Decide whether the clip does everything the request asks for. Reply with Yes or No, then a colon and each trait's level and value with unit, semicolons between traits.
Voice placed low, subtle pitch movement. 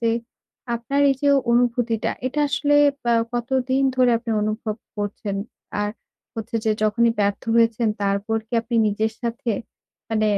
No: high, 230 Hz; narrow, 2.3 semitones